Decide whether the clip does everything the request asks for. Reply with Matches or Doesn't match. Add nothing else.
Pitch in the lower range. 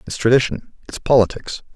Matches